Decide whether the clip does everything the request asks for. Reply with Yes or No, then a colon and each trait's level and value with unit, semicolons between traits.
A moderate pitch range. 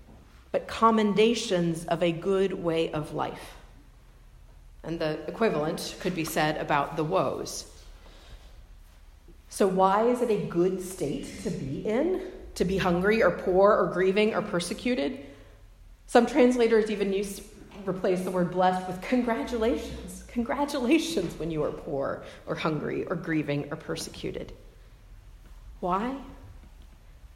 No: wide, 5.8 semitones